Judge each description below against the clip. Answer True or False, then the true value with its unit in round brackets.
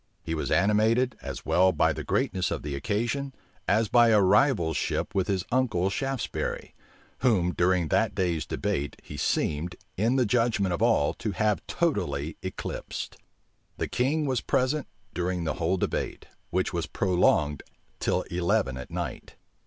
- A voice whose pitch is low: True (95 Hz)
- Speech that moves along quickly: False (155 wpm)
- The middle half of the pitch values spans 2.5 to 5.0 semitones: False (5.5 semitones)